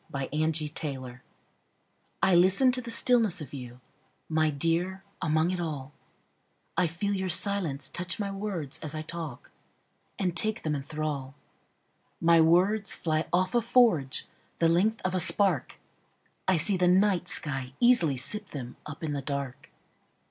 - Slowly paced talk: Yes, slow, 130 wpm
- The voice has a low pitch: No, medium, 165 Hz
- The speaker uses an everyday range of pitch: Yes, average, 4.8 semitones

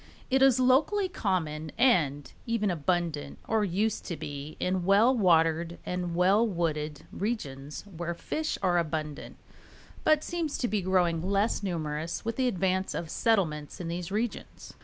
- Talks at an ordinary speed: Yes, average, 150 wpm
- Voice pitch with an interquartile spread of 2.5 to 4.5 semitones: No, wide, 5.4 semitones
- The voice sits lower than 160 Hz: No, medium, 180 Hz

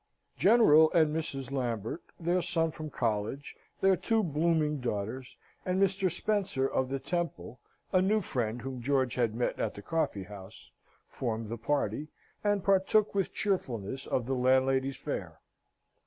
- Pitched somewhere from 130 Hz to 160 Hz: Yes, medium, 140 Hz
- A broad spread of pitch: Yes, wide, 6.5 semitones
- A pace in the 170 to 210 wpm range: No, average, 150 wpm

